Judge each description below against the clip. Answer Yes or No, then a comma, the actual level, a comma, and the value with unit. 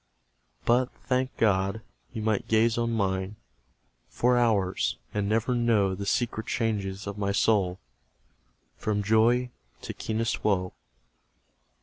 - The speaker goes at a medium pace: No, slow, 120 wpm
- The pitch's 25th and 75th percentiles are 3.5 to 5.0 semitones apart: No, average, 2.9 semitones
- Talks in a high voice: No, low, 110 Hz